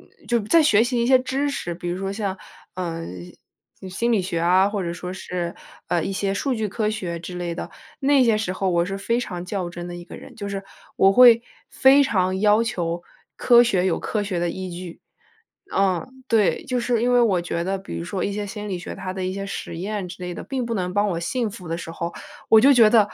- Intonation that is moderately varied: Yes, average, 4.4 semitones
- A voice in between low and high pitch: No, high, 195 Hz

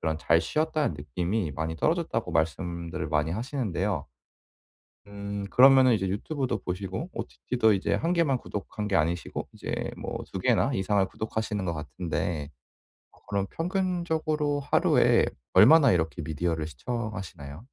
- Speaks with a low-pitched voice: Yes, low, 100 Hz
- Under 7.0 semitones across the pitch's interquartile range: No, wide, 7.7 semitones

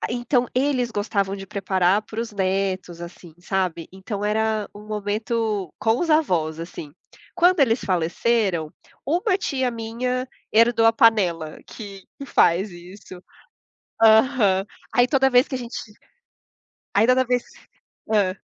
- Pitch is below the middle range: No, high, 215 Hz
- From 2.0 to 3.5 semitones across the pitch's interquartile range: No, average, 4.5 semitones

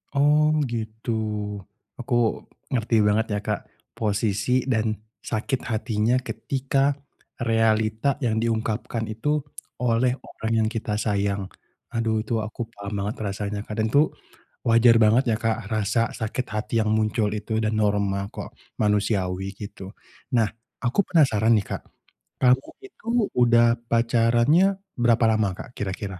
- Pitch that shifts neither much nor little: No, narrow, 2.1 semitones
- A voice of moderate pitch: No, low, 110 Hz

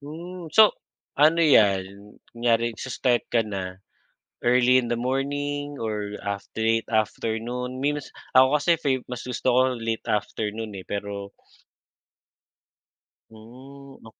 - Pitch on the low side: Yes, low, 120 Hz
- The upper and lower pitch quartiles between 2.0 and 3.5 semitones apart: No, average, 4.1 semitones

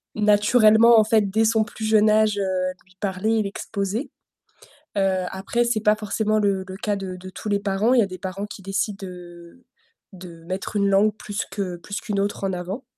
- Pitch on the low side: No, high, 200 Hz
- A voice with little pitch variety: Yes, narrow, 2.3 semitones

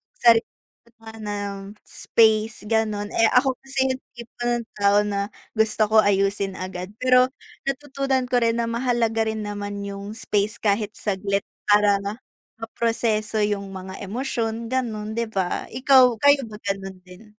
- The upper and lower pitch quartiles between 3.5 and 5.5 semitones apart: No, narrow, 2.6 semitones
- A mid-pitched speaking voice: No, high, 215 Hz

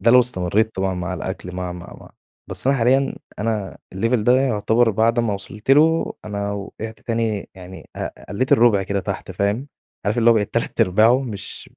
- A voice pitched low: Yes, low, 110 Hz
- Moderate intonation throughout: Yes, average, 3.3 semitones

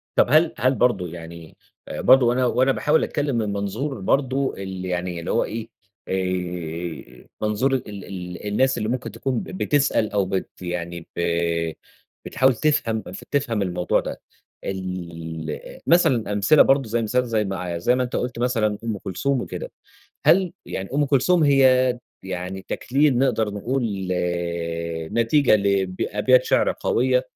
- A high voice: No, low, 110 Hz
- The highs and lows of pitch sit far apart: Yes, wide, 5.8 semitones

